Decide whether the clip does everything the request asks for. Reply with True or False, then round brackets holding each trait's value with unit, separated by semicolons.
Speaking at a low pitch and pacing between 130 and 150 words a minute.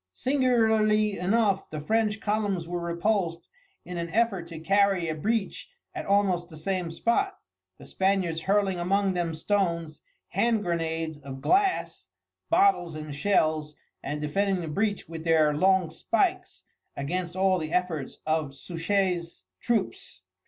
False (180 Hz; 140 wpm)